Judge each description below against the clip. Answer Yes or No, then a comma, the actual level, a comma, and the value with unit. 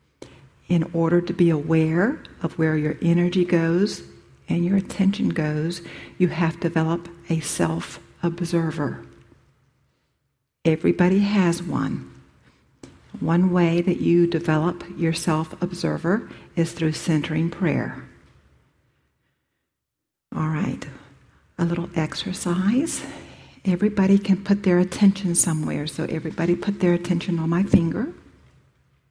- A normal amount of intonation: No, narrow, 2.2 semitones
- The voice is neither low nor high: Yes, medium, 170 Hz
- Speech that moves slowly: Yes, slow, 115 wpm